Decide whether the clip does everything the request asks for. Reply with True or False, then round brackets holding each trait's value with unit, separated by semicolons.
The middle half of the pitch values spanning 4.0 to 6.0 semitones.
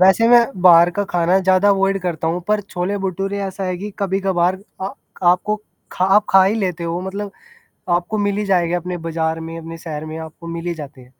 False (2.7 semitones)